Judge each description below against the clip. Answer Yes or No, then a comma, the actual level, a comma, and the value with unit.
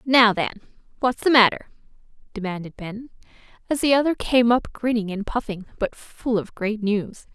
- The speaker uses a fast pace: No, average, 165 wpm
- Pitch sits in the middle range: No, high, 225 Hz